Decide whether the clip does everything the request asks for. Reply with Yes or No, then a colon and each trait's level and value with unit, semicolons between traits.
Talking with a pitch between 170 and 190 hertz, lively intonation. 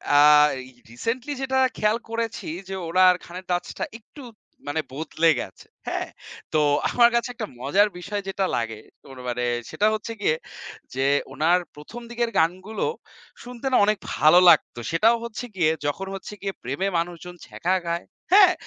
Yes: medium, 185 Hz; wide, 6.1 semitones